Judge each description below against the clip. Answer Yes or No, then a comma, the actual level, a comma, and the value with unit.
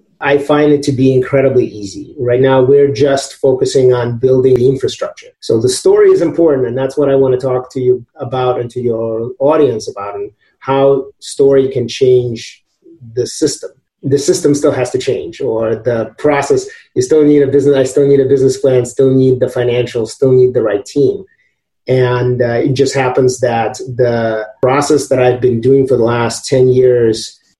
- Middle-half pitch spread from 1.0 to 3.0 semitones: Yes, narrow, 2.6 semitones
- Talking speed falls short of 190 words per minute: No, average, 195 wpm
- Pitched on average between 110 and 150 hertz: Yes, low, 135 Hz